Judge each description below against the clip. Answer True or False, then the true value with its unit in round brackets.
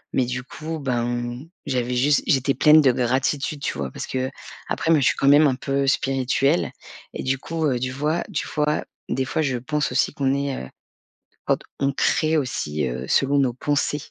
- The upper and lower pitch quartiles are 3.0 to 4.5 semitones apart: False (2.6 semitones)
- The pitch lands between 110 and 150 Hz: True (135 Hz)